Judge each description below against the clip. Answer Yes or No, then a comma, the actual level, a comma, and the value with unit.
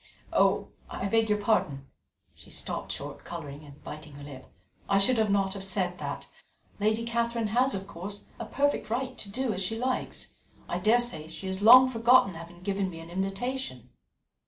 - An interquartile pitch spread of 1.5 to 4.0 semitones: No, average, 5.0 semitones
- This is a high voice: Yes, high, 200 Hz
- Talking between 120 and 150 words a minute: No, average, 180 wpm